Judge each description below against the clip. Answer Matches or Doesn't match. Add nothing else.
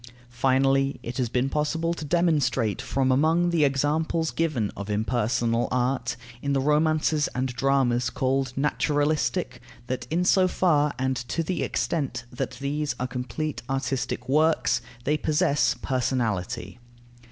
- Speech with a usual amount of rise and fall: Matches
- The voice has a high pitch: Doesn't match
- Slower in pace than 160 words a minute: Matches